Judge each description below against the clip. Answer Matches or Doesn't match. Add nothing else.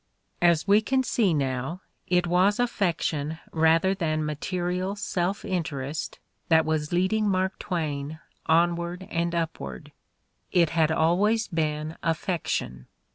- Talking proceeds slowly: Matches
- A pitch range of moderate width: Matches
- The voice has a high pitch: Doesn't match